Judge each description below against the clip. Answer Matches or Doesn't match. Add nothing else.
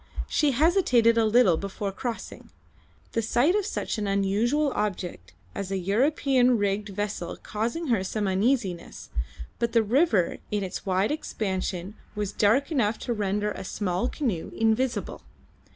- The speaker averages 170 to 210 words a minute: Doesn't match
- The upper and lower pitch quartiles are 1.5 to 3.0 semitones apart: Doesn't match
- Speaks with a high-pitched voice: Matches